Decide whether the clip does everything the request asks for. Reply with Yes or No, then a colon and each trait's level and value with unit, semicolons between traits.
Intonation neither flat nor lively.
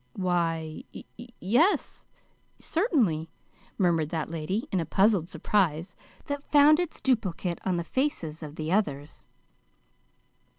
No: wide, 6.1 semitones